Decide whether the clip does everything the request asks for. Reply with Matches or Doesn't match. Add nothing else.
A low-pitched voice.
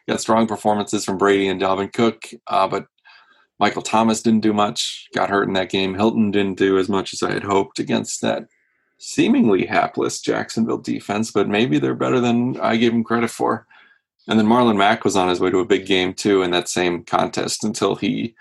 Matches